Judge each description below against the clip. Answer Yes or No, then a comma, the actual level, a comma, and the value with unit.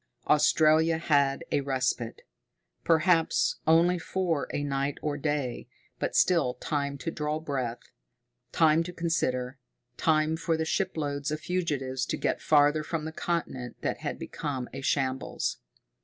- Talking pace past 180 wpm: No, average, 140 wpm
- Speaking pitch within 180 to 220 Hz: No, medium, 150 Hz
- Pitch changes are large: No, average, 3.0 semitones